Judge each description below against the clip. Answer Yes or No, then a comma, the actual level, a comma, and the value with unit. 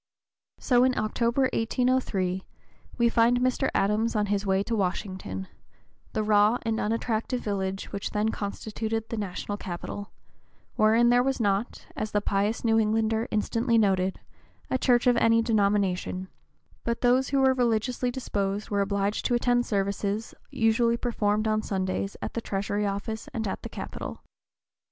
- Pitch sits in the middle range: No, high, 215 Hz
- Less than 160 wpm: Yes, average, 150 wpm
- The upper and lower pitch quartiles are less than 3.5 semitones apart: Yes, average, 2.8 semitones